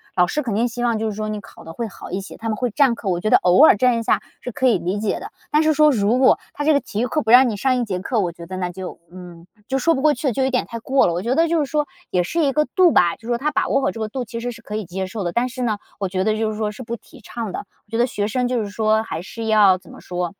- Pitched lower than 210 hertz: No, high, 225 Hz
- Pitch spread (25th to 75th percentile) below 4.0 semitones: No, average, 4.4 semitones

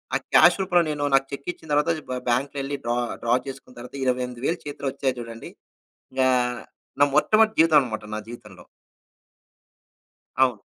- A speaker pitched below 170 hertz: Yes, low, 135 Hz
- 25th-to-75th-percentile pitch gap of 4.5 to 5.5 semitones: No, average, 3.4 semitones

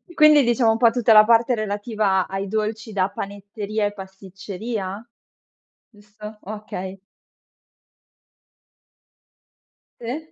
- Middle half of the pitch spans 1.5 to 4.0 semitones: Yes, narrow, 2.4 semitones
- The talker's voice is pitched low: No, high, 210 Hz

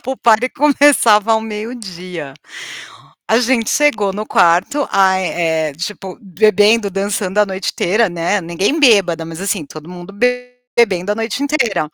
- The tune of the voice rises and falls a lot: No, average, 4.2 semitones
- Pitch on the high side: Yes, high, 200 Hz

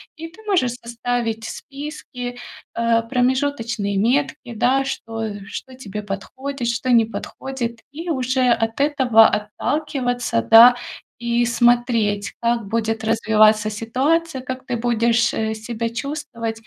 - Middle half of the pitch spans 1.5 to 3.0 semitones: Yes, average, 2.7 semitones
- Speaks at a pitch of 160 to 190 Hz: No, high, 235 Hz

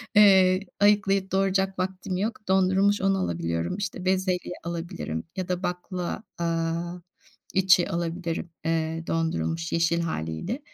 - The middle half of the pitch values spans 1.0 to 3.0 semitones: Yes, narrow, 2.5 semitones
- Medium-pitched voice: Yes, medium, 180 Hz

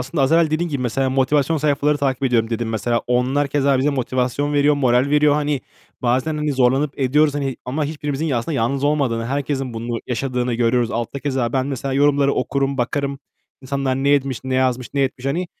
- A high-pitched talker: No, low, 135 Hz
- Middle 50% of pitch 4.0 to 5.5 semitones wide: No, narrow, 2.4 semitones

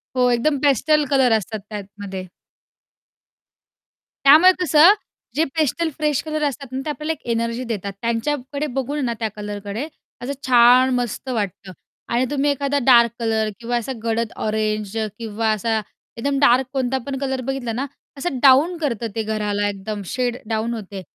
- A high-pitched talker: Yes, high, 245 Hz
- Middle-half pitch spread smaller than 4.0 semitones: No, average, 4.3 semitones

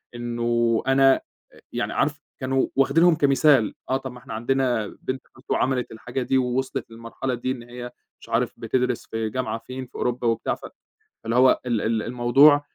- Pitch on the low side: Yes, low, 125 Hz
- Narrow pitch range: Yes, narrow, 2.1 semitones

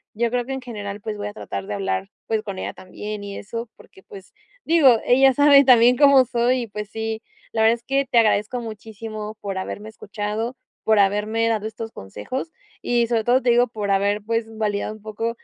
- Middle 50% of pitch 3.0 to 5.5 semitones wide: No, narrow, 2.6 semitones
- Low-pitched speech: No, high, 220 Hz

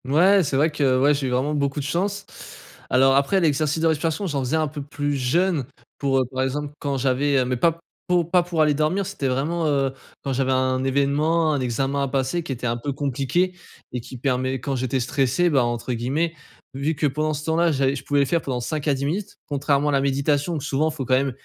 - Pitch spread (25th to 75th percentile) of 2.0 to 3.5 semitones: Yes, average, 2.9 semitones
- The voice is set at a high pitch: No, medium, 140 Hz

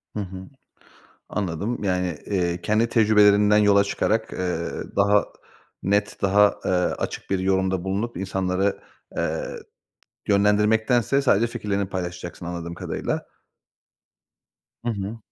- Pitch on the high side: No, low, 100 Hz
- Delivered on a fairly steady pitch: Yes, narrow, 2.3 semitones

